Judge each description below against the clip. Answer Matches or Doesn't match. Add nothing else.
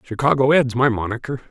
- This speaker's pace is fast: Doesn't match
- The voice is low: Matches